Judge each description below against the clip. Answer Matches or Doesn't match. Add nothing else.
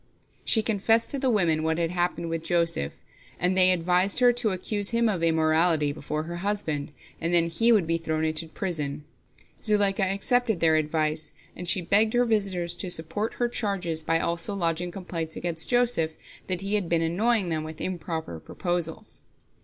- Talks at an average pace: Matches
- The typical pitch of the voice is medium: Matches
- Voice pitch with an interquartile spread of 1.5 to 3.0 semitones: Doesn't match